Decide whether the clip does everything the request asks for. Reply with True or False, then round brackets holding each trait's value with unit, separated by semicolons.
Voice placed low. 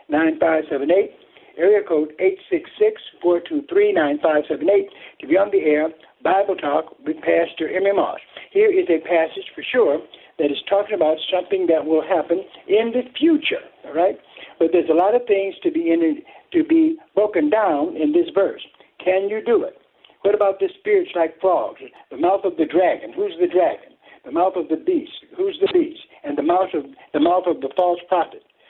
False (205 Hz)